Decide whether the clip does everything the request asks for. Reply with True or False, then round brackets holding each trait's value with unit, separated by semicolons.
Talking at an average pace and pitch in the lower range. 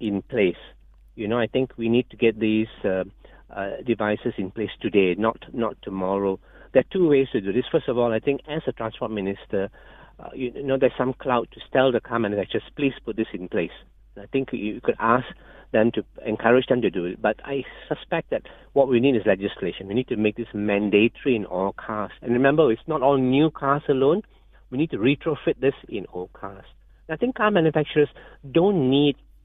False (210 wpm; 120 Hz)